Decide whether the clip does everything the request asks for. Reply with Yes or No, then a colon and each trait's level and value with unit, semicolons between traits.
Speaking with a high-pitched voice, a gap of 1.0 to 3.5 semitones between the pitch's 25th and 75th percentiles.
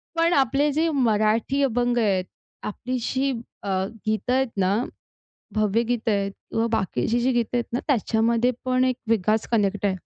Yes: high, 230 Hz; average, 3.2 semitones